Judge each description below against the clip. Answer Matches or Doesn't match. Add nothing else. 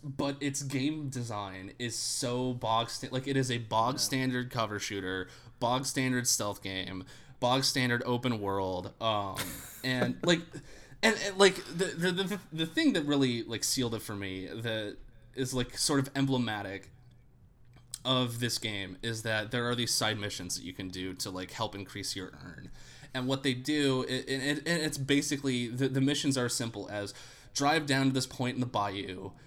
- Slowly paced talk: Doesn't match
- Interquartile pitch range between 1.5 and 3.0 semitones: Doesn't match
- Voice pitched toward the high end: Doesn't match